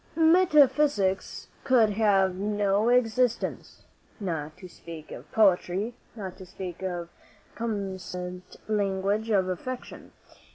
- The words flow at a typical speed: No, slow, 110 wpm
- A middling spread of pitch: Yes, average, 3.6 semitones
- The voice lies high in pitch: Yes, high, 200 Hz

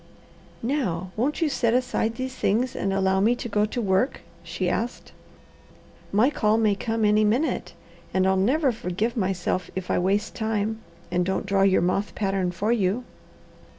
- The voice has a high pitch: Yes, high, 210 Hz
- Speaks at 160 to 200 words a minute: Yes, average, 170 wpm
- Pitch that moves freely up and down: No, average, 3.7 semitones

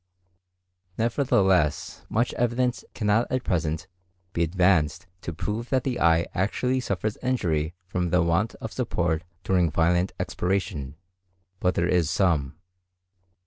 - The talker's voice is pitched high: No, very low, 90 Hz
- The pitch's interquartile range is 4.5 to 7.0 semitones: Yes, average, 5.1 semitones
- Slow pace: Yes, slow, 125 wpm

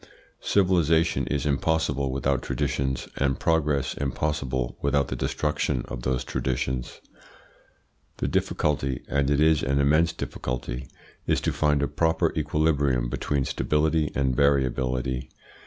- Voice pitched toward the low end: Yes, very low, 70 Hz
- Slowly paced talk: Yes, slow, 125 wpm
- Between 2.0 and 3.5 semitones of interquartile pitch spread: Yes, average, 2.7 semitones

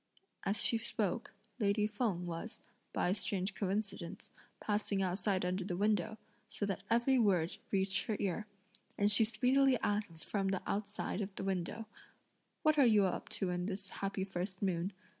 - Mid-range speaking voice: No, high, 200 Hz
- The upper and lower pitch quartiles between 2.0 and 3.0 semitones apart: Yes, narrow, 2.5 semitones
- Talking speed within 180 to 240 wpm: No, average, 160 wpm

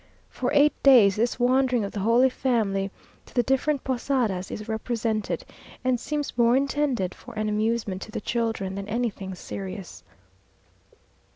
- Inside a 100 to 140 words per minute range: No, average, 150 wpm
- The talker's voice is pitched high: Yes, high, 230 Hz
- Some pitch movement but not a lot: Yes, average, 3.9 semitones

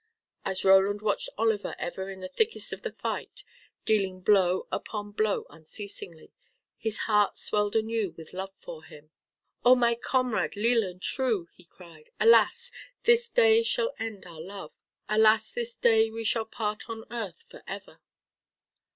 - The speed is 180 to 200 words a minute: No, average, 155 wpm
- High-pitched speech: Yes, high, 215 Hz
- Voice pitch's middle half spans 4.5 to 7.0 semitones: No, average, 3.3 semitones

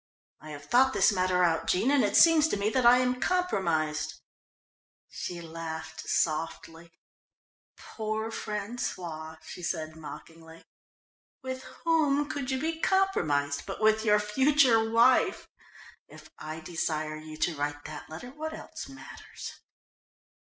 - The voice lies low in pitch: No, high, 200 Hz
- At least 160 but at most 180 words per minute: No, slow, 135 wpm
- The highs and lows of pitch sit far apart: Yes, wide, 8.4 semitones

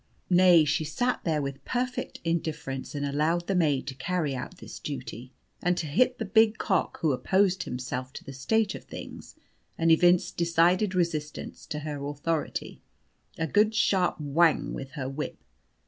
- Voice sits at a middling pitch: Yes, medium, 165 Hz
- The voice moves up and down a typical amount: Yes, average, 4.3 semitones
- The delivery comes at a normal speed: Yes, average, 165 wpm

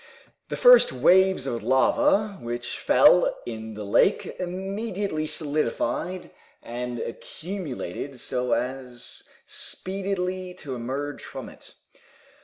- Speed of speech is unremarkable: No, slow, 100 wpm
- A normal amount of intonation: No, wide, 7.3 semitones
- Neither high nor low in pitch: Yes, medium, 150 Hz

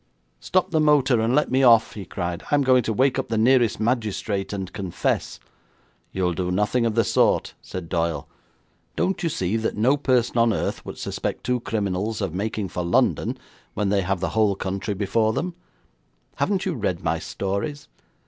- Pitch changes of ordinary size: Yes, average, 4.7 semitones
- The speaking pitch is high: No, low, 110 Hz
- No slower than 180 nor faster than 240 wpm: Yes, average, 185 wpm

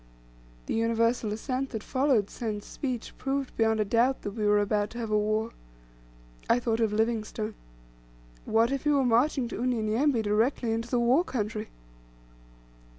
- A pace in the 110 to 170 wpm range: Yes, average, 160 wpm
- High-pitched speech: Yes, high, 230 Hz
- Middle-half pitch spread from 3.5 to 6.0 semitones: No, average, 2.8 semitones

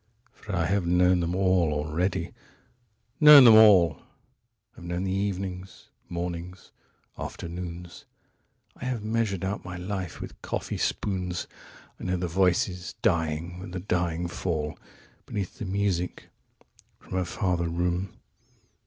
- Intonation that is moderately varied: No, narrow, 2.1 semitones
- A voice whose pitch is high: No, very low, 90 Hz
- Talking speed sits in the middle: No, slow, 120 wpm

